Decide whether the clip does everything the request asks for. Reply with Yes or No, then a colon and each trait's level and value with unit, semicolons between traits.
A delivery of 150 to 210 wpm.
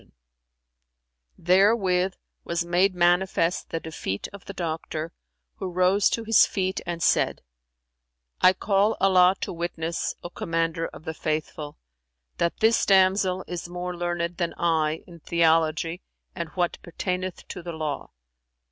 No: average, 140 wpm